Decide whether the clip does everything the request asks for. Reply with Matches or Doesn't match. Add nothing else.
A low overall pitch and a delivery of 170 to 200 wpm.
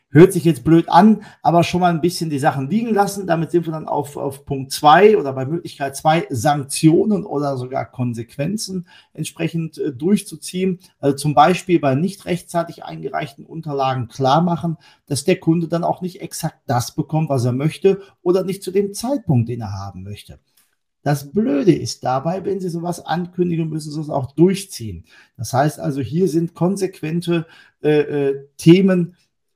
Doesn't match